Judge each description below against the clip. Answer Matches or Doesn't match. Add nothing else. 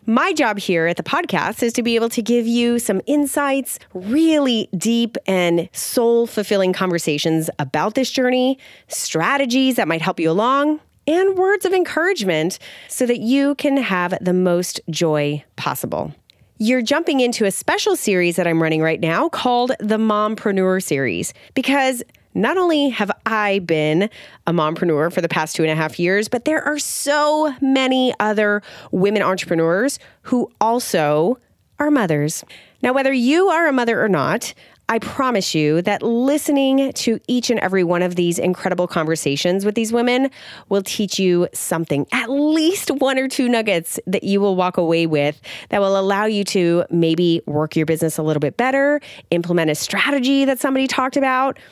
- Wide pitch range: Matches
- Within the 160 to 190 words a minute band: Matches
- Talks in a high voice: Matches